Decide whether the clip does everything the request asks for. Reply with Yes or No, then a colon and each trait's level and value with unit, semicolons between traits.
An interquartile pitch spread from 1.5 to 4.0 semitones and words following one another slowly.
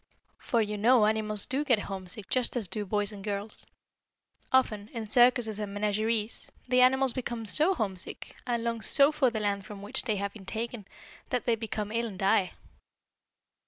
No: average, 2.9 semitones; average, 180 wpm